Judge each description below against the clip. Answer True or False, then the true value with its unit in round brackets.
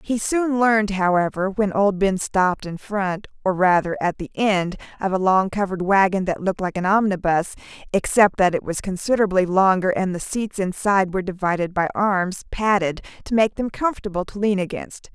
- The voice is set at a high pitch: True (195 Hz)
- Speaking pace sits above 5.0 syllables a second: True (5.4 syllables/s)